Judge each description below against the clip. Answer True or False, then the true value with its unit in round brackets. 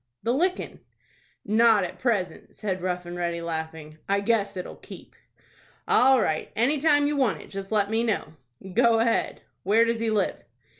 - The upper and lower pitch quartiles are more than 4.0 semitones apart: True (4.5 semitones)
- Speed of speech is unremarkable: True (170 wpm)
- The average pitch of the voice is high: True (215 Hz)